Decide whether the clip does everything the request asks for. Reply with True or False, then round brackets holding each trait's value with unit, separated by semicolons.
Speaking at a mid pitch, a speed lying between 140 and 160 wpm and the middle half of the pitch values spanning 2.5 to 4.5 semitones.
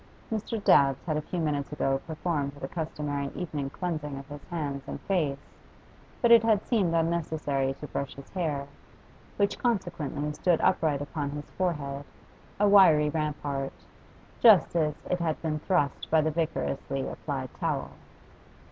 True (150 Hz; 150 wpm; 3.6 semitones)